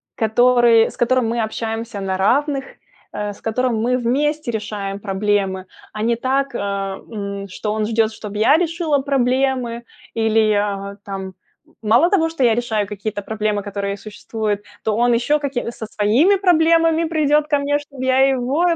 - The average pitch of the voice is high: Yes, high, 230 Hz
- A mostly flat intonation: No, average, 4.7 semitones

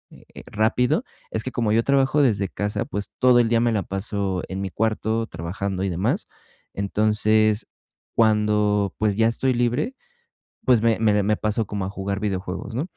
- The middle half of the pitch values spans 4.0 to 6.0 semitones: No, narrow, 2.5 semitones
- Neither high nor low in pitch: No, low, 105 Hz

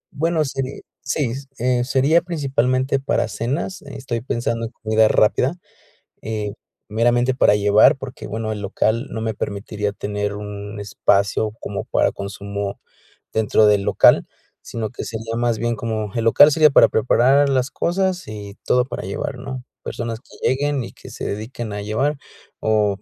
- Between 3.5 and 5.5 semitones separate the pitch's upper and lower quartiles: Yes, average, 4.0 semitones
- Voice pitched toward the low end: Yes, low, 115 Hz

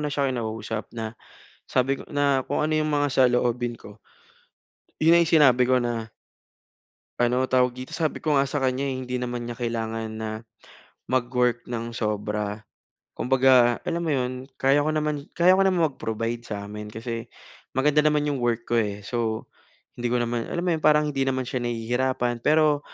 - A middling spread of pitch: Yes, average, 3.6 semitones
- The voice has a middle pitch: No, low, 125 Hz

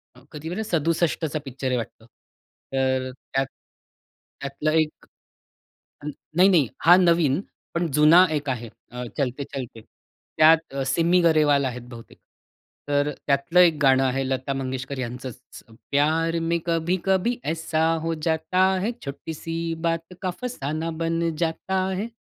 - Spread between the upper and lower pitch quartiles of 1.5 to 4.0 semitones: Yes, average, 3.7 semitones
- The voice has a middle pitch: Yes, medium, 155 Hz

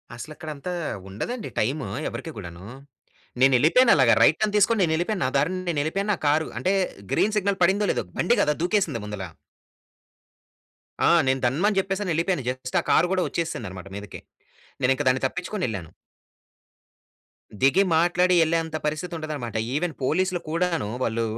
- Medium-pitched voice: Yes, medium, 160 Hz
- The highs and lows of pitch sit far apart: Yes, wide, 6.1 semitones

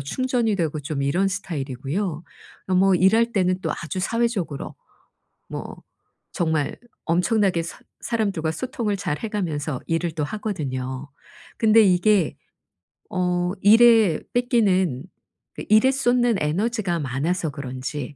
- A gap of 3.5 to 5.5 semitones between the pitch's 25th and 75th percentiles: No, wide, 6.0 semitones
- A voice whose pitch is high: No, medium, 180 Hz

